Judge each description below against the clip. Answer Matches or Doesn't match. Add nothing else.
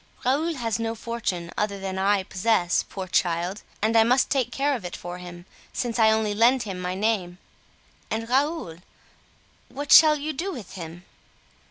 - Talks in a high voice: Matches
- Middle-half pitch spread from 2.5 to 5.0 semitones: Doesn't match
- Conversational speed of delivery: Matches